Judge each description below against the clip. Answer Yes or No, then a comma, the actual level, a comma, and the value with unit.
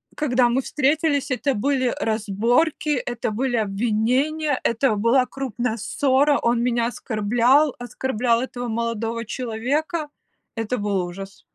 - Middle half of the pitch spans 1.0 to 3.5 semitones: Yes, average, 3.2 semitones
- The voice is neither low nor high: No, high, 245 Hz